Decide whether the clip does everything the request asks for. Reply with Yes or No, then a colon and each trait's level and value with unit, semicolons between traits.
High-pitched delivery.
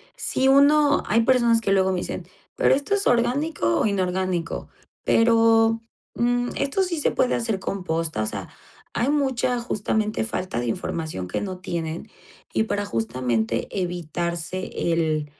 Yes: high, 205 Hz